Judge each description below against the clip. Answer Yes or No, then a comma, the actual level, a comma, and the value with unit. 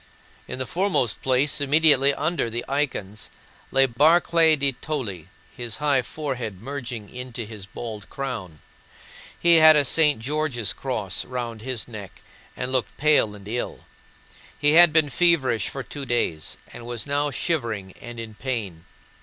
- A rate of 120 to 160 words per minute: Yes, average, 150 wpm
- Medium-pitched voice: No, low, 130 Hz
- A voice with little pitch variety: No, average, 4.6 semitones